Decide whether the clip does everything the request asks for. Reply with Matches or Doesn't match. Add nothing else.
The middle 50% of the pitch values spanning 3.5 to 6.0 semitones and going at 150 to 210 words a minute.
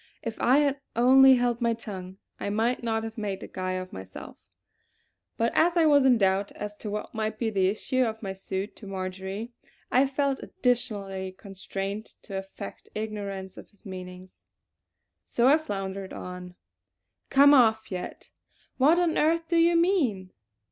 Matches